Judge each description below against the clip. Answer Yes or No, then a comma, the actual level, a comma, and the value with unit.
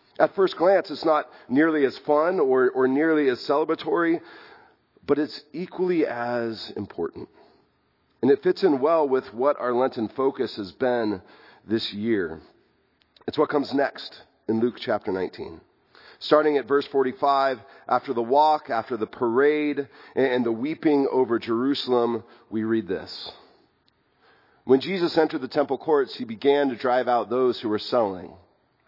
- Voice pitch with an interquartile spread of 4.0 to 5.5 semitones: Yes, average, 5.1 semitones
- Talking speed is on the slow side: No, average, 150 wpm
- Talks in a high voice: No, low, 135 Hz